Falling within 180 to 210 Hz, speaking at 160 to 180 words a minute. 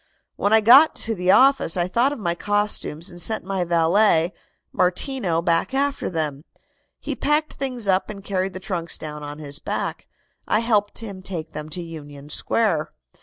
Yes: medium, 185 Hz; average, 175 wpm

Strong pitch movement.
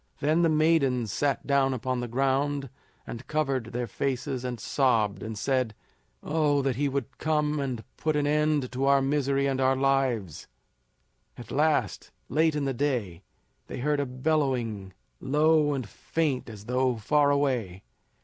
No: average, 3.1 semitones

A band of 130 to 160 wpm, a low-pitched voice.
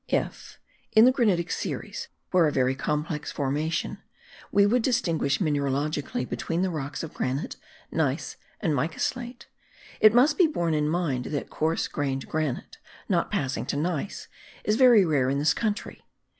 No: average, 155 wpm; medium, 160 Hz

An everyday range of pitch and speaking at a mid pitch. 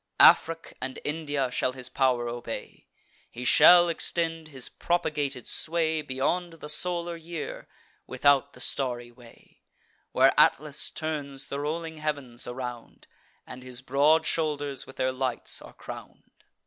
Yes: average, 3.7 semitones; medium, 145 Hz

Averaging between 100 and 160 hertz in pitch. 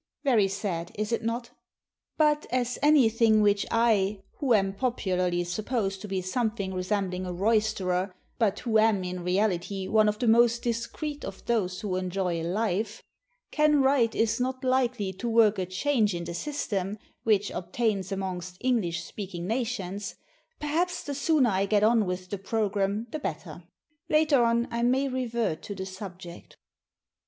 No: high, 210 Hz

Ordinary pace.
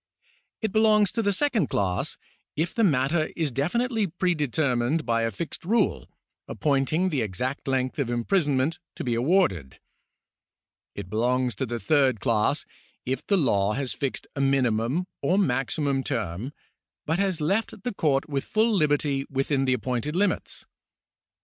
Yes: average, 150 wpm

